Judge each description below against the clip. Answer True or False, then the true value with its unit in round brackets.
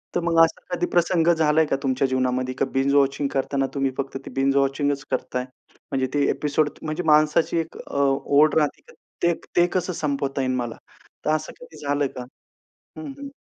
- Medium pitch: True (145 Hz)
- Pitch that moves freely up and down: False (2.9 semitones)